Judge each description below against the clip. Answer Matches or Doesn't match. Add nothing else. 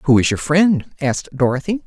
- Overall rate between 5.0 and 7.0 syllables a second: Matches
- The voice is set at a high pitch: Doesn't match